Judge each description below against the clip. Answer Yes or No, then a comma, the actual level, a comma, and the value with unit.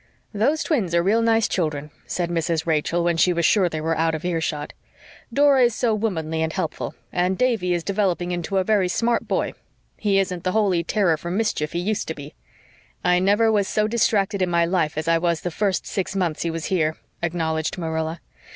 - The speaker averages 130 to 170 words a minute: No, fast, 205 wpm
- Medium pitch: Yes, medium, 180 Hz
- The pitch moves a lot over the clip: No, average, 3.9 semitones